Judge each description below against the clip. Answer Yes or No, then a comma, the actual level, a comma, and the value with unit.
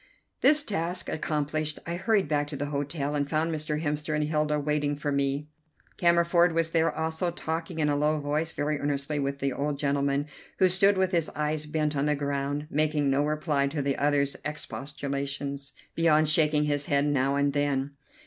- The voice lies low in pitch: No, medium, 150 Hz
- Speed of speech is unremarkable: Yes, average, 185 wpm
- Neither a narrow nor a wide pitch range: No, narrow, 2.0 semitones